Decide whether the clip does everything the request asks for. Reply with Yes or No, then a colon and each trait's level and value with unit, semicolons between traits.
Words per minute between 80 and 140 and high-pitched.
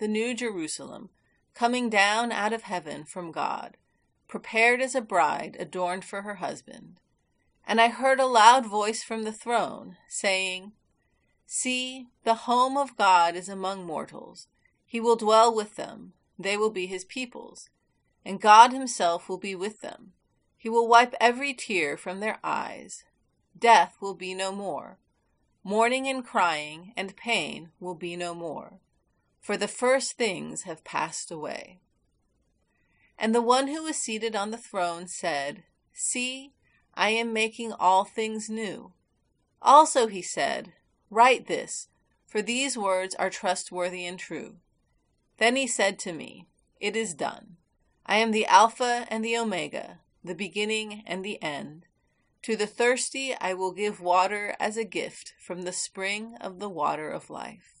No: average, 155 wpm; high, 215 Hz